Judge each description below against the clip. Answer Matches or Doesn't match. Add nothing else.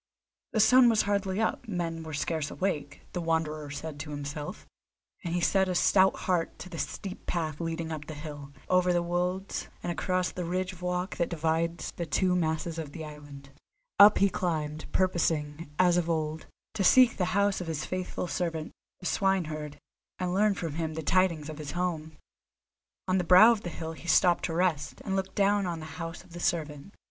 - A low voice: Doesn't match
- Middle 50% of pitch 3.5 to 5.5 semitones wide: Doesn't match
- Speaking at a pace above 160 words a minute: Matches